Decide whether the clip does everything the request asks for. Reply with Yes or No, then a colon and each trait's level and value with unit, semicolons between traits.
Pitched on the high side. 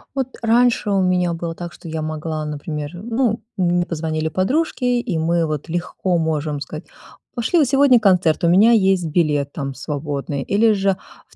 No: medium, 175 Hz